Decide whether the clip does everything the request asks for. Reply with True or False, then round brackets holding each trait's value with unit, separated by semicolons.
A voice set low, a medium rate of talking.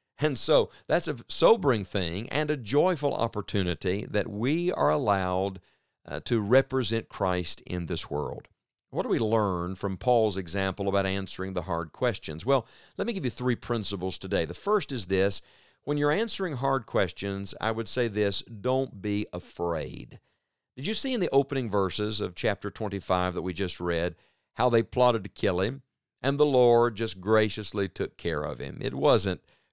True (105 Hz; 180 wpm)